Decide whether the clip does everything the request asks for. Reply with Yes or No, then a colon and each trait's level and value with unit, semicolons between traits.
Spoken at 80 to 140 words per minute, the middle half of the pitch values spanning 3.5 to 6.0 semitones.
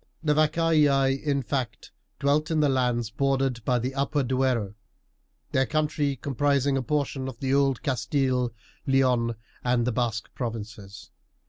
No: slow, 135 wpm; narrow, 2.5 semitones